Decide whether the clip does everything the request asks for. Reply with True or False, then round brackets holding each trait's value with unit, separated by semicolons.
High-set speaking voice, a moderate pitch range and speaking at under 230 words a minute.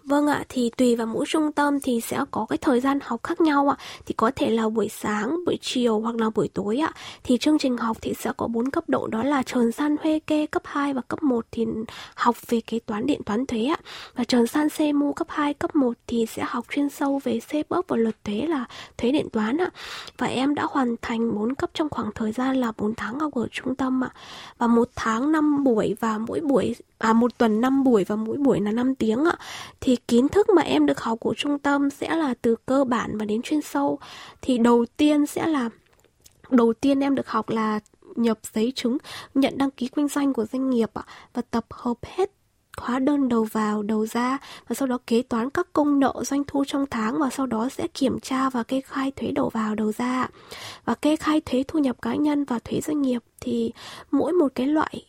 False (255 Hz; 4.0 semitones; 240 wpm)